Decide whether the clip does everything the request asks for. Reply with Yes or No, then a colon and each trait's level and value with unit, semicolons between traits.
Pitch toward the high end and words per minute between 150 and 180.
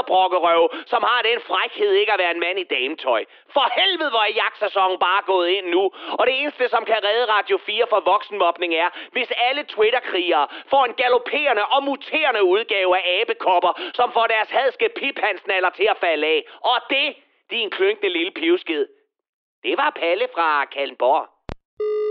Yes: very high, 295 Hz; average, 170 wpm